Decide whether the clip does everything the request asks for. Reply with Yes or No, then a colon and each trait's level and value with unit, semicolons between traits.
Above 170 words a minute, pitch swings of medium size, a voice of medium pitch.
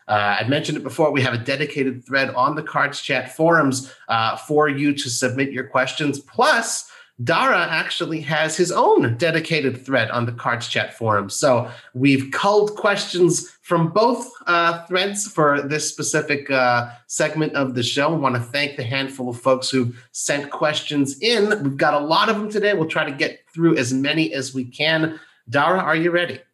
Yes: average, 190 wpm; average, 3.8 semitones; medium, 145 Hz